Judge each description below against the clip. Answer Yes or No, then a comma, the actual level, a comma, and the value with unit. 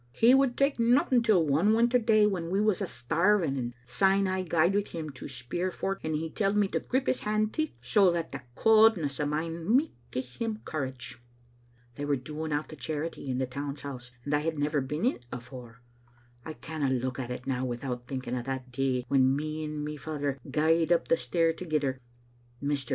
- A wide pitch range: Yes, wide, 6.6 semitones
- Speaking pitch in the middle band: Yes, medium, 155 Hz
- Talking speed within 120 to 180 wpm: No, fast, 205 wpm